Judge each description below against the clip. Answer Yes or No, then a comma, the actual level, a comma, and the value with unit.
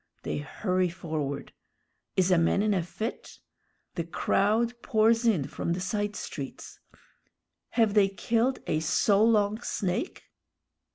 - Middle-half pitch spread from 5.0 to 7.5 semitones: No, average, 4.2 semitones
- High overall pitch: Yes, high, 200 Hz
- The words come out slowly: Yes, slow, 130 wpm